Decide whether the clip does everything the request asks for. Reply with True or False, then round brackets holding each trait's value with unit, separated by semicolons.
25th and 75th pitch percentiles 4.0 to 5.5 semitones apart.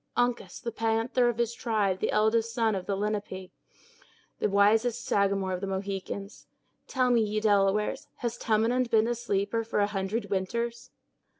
False (2.8 semitones)